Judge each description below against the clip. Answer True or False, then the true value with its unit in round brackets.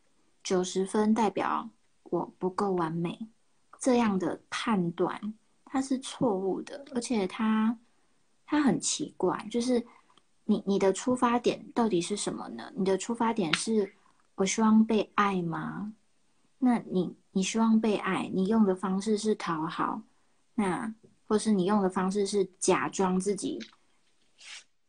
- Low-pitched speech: False (210 Hz)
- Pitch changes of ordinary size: True (3.3 semitones)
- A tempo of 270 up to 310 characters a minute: False (195 characters per minute)